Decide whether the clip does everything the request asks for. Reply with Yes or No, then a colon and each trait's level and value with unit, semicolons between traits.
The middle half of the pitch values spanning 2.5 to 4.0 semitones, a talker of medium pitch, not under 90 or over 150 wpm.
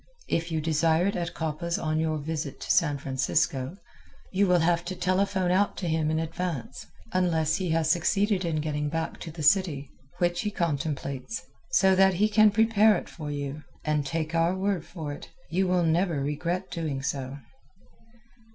No: average, 3.3 semitones; medium, 165 Hz; average, 180 wpm